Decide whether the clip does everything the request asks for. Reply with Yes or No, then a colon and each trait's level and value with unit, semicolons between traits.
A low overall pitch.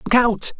No: high, 230 Hz